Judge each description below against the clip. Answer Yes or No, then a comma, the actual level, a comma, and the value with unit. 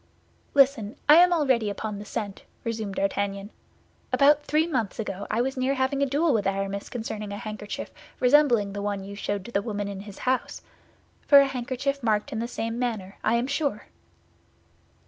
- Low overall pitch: No, high, 230 Hz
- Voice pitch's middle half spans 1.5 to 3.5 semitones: No, average, 4.9 semitones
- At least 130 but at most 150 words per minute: No, average, 180 wpm